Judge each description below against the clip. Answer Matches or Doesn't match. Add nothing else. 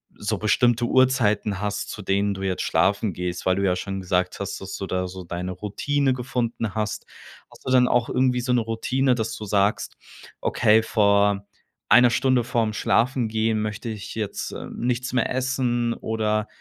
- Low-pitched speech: Matches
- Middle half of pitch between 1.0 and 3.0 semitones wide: Doesn't match